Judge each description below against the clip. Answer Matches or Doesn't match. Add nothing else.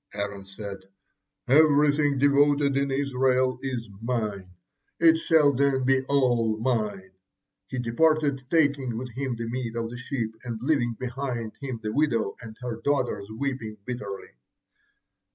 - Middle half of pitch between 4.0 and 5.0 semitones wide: Doesn't match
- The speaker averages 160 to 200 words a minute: Doesn't match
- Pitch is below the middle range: Matches